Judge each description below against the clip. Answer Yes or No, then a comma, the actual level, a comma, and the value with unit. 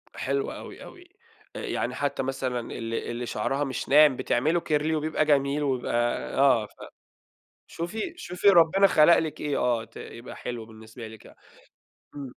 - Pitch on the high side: No, medium, 140 Hz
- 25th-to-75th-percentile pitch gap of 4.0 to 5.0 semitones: Yes, average, 4.6 semitones